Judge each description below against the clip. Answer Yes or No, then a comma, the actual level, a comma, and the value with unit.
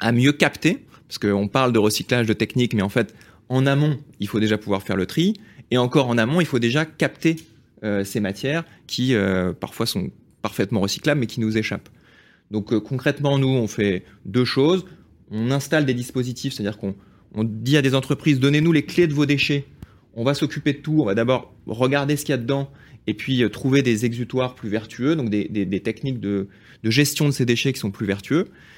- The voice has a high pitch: No, low, 125 Hz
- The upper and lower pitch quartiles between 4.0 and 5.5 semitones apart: Yes, average, 4.8 semitones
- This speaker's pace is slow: No, fast, 220 wpm